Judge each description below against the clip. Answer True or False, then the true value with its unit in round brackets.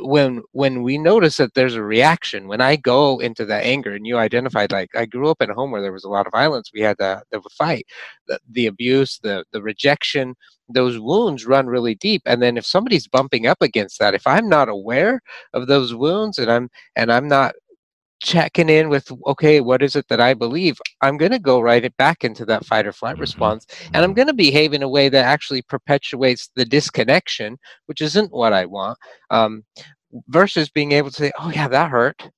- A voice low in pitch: True (130 Hz)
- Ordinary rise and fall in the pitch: True (3.9 semitones)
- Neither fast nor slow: False (220 wpm)